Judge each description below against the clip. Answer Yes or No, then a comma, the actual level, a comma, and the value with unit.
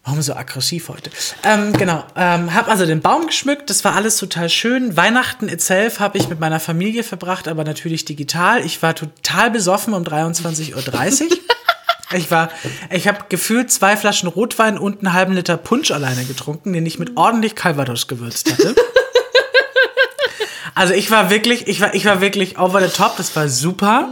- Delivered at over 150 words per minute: Yes, average, 180 wpm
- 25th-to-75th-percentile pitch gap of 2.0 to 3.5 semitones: No, wide, 5.5 semitones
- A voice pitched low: No, high, 190 Hz